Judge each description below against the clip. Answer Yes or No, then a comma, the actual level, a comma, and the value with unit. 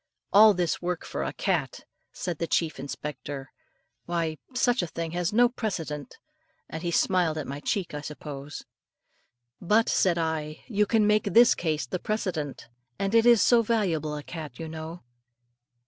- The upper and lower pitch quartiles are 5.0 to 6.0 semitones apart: Yes, wide, 5.4 semitones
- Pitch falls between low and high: Yes, medium, 170 Hz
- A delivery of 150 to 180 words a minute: Yes, average, 165 wpm